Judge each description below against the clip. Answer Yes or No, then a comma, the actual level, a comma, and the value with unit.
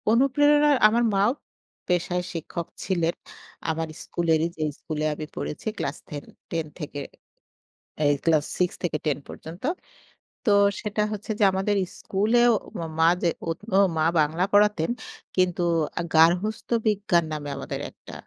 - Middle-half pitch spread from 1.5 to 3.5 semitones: No, average, 4.6 semitones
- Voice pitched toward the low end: No, medium, 175 Hz